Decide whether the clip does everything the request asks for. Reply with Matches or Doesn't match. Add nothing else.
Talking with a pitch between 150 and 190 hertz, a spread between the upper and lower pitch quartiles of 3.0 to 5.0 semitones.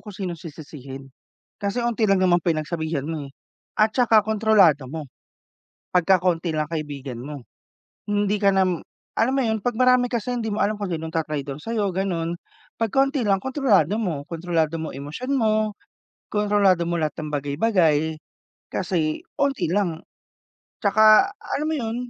Doesn't match